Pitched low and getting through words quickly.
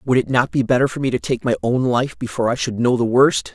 Yes: low, 125 Hz; fast, 305 wpm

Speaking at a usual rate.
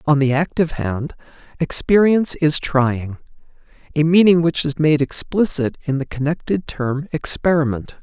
No: slow, 125 wpm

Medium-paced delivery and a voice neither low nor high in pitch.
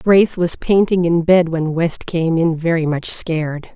Yes: average, 190 wpm; medium, 165 Hz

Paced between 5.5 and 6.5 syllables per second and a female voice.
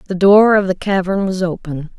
No: 5.1 syllables/s; female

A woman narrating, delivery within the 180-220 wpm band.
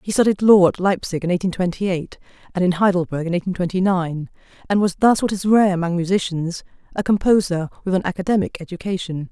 Yes: female; average, 185 wpm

